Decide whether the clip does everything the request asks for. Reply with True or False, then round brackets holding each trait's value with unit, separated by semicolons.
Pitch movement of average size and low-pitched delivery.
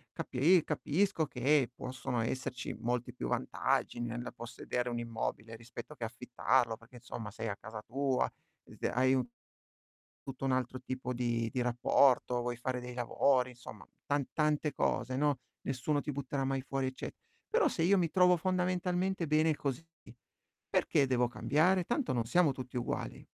True (3.7 semitones; 130 Hz)